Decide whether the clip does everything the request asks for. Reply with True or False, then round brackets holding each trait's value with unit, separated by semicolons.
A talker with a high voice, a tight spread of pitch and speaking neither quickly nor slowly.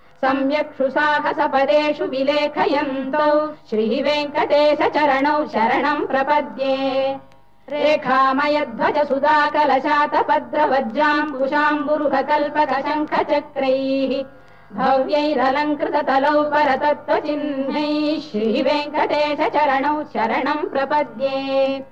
False (295 Hz; 1.8 semitones; 50 wpm)